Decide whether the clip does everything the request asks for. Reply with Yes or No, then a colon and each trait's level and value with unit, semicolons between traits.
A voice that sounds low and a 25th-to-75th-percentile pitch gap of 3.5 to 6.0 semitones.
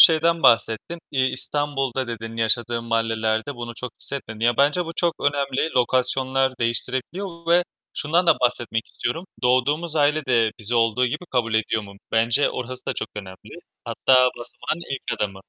Yes: low, 125 Hz; average, 4.1 semitones